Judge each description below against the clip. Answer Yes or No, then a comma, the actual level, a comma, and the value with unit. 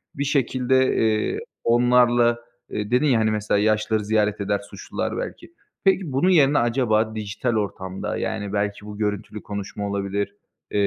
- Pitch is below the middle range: Yes, low, 110 Hz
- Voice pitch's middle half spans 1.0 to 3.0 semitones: No, average, 3.4 semitones